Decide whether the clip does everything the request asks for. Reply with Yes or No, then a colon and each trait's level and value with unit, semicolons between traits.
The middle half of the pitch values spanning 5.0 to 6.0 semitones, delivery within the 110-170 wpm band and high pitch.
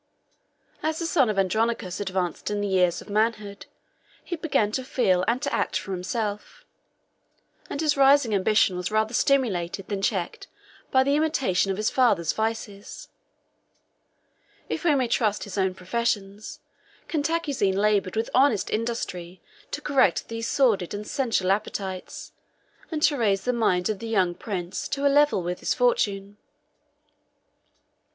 Yes: average, 5.3 semitones; average, 150 wpm; high, 215 Hz